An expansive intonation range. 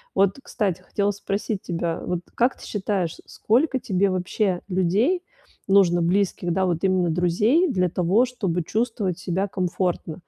No: average, 2.8 semitones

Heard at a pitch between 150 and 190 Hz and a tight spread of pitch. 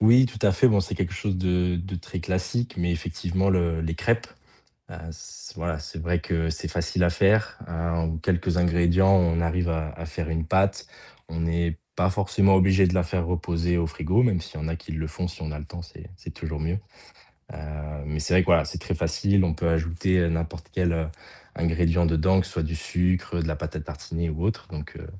No: very low, 85 Hz; narrow, 2.1 semitones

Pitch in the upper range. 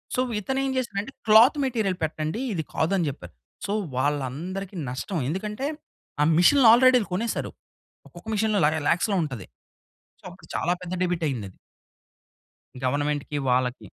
No: medium, 180 Hz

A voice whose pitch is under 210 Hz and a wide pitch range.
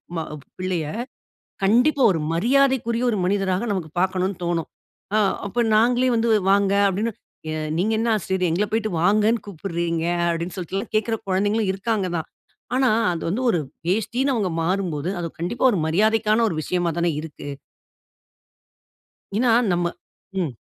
No: high, 195 Hz; average, 4.4 semitones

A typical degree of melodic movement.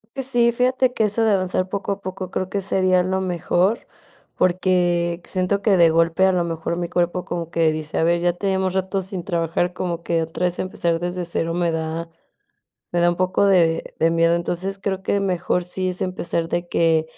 No: narrow, 1.9 semitones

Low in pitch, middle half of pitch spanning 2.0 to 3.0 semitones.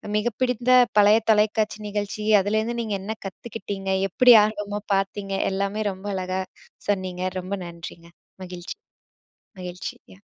No: high, 205 Hz; narrow, 2.4 semitones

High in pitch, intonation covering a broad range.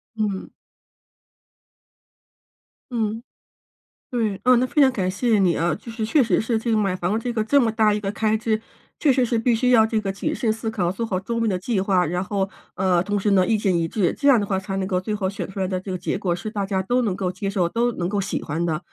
No: high, 205 Hz; average, 3.2 semitones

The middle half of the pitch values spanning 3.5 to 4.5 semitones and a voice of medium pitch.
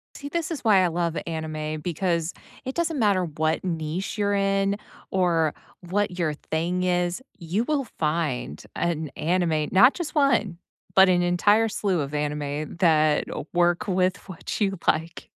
Yes: average, 4.0 semitones; medium, 175 Hz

